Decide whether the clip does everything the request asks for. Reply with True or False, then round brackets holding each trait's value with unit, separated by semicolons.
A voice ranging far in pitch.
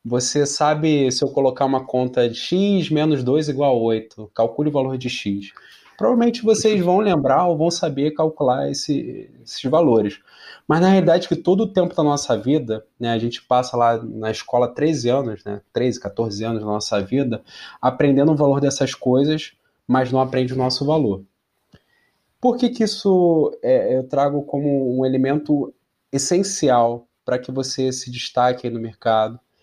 False (4.5 semitones)